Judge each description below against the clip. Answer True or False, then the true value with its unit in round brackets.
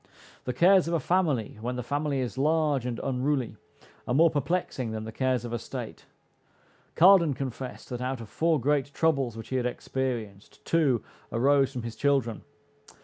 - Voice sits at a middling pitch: False (130 Hz)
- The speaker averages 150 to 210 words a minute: True (175 wpm)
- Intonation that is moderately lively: True (3.6 semitones)